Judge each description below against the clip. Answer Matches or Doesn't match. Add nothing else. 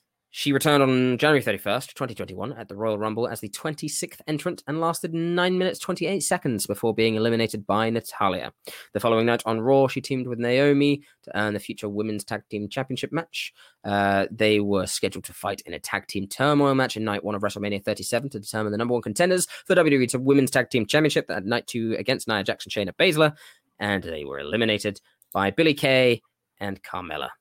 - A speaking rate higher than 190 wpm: Matches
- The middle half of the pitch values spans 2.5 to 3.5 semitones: Doesn't match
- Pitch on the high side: Doesn't match